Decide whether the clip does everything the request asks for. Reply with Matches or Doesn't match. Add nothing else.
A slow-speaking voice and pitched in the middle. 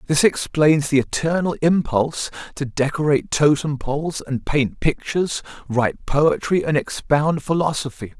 Matches